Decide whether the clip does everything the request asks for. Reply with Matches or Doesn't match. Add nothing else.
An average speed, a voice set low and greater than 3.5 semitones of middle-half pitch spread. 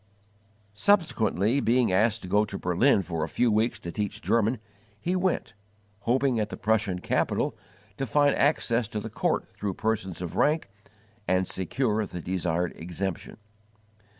Matches